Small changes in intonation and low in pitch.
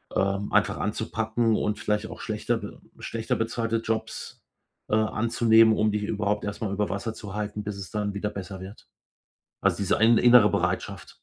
Yes: narrow, 1.6 semitones; low, 105 Hz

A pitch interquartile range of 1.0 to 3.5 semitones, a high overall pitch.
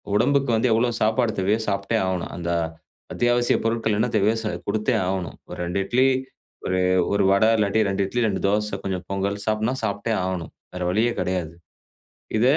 No: average, 2.9 semitones; low, 105 Hz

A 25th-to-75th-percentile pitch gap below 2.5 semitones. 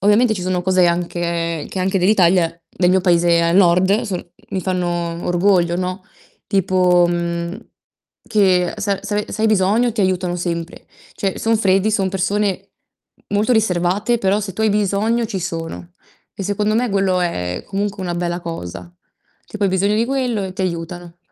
No: average, 2.9 semitones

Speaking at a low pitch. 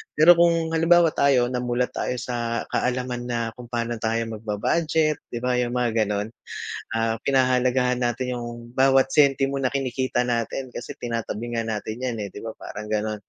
Yes: low, 125 Hz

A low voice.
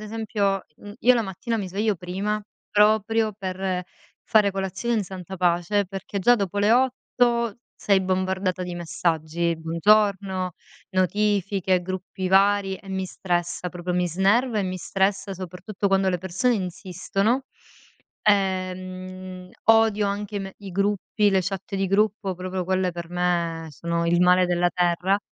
No: high, 190 Hz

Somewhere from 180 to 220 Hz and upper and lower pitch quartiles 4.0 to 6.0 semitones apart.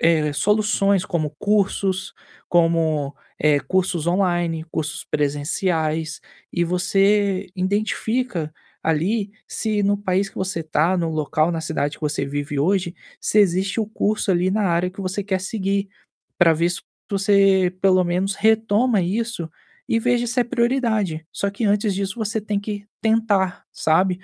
No: high, 190 Hz; average, 3.6 semitones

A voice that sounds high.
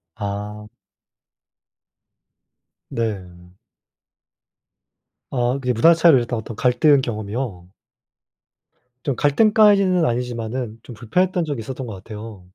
No: low, 120 Hz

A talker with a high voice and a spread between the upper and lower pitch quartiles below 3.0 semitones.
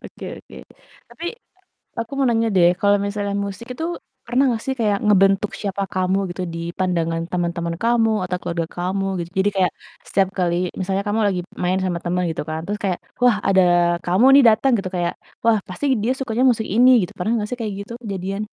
No: high, 195 Hz; average, 3.6 semitones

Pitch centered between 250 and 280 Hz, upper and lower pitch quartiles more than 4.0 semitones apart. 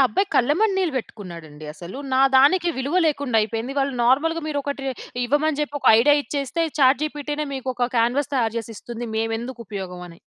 Yes: very high, 265 Hz; average, 4.6 semitones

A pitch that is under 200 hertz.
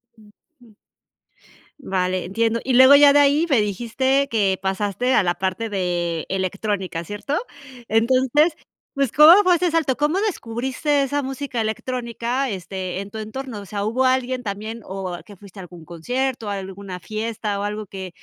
No: high, 225 Hz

